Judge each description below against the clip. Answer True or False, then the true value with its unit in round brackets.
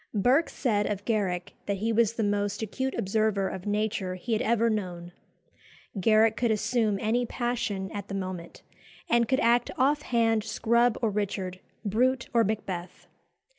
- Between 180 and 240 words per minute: False (160 wpm)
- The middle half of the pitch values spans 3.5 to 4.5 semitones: False (3.0 semitones)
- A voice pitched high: True (215 Hz)